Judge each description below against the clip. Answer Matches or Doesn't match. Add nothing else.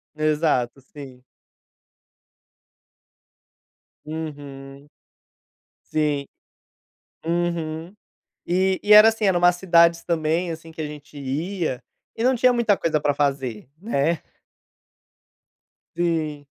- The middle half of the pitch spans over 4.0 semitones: Doesn't match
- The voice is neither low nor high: Matches